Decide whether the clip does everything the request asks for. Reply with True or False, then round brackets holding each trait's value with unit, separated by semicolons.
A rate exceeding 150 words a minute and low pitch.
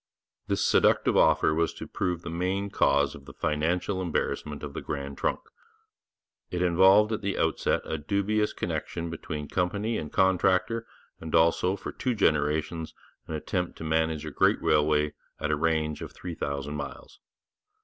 True (160 wpm; 80 Hz)